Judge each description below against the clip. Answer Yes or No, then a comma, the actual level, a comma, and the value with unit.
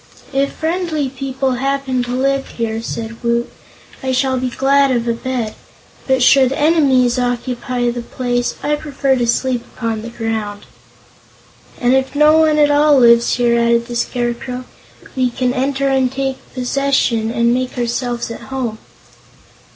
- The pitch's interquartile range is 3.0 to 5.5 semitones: No, narrow, 2.4 semitones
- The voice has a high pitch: Yes, very high, 255 Hz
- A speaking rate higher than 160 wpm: No, average, 155 wpm